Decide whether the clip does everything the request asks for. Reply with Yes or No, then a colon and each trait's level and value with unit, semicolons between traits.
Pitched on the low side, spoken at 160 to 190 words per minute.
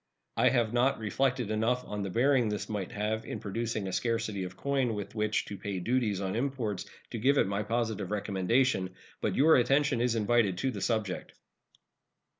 Yes: low, 110 Hz; average, 185 wpm